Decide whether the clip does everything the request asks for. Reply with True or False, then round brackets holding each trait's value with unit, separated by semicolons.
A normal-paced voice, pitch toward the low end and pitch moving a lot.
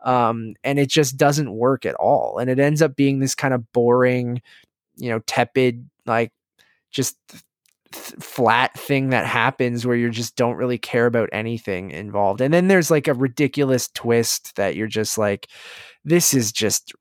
False (175 wpm; 125 Hz; 2.9 semitones)